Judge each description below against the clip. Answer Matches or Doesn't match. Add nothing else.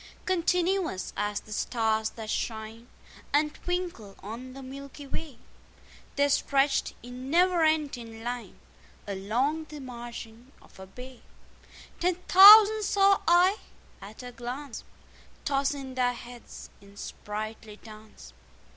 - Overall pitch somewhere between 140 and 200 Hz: Doesn't match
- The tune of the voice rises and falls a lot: Matches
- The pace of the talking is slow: Matches